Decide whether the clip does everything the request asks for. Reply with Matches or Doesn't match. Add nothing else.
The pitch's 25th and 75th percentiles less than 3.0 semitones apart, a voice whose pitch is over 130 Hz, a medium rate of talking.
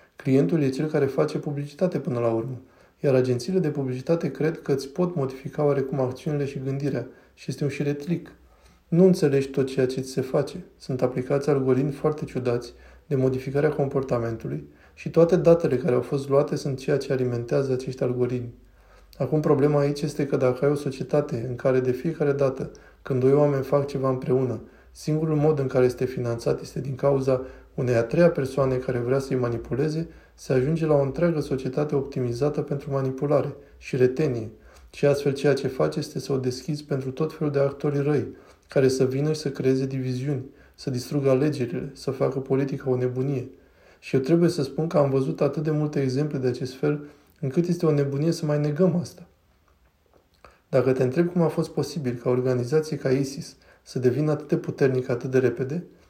Doesn't match